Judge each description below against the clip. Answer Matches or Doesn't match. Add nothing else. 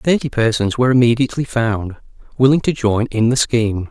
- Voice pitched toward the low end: Matches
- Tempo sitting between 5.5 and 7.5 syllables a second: Matches